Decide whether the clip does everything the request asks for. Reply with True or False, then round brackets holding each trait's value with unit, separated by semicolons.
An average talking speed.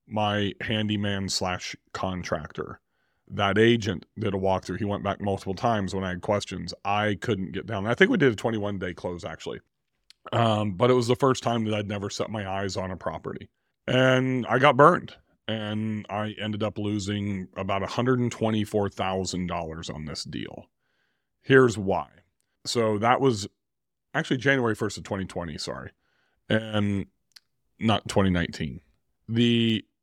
True (150 wpm)